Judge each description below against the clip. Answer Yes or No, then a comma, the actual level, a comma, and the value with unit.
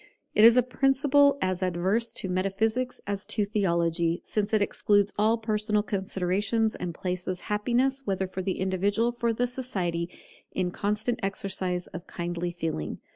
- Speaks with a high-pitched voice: Yes, high, 200 Hz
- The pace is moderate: Yes, average, 150 wpm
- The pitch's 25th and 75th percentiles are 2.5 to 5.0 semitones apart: Yes, average, 3.8 semitones